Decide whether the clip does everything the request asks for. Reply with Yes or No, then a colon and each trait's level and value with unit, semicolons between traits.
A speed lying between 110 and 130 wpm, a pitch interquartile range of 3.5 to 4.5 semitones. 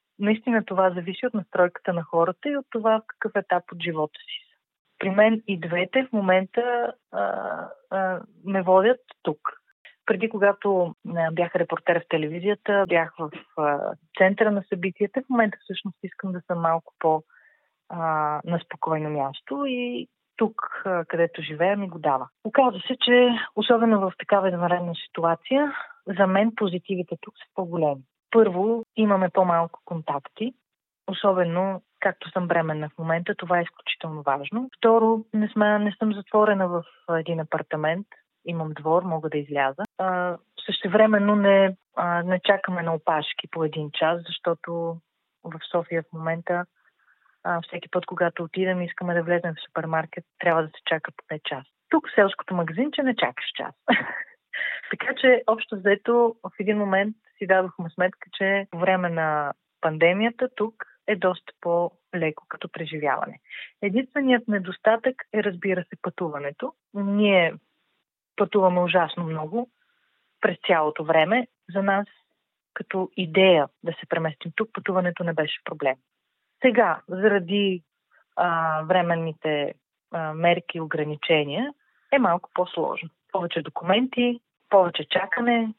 No: average, 140 wpm; average, 4.1 semitones